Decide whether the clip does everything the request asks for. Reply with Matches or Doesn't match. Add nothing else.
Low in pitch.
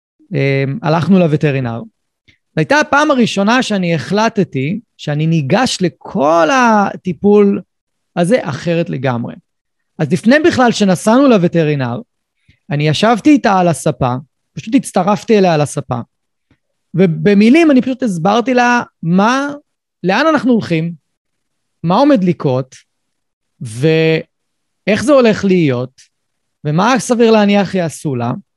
Doesn't match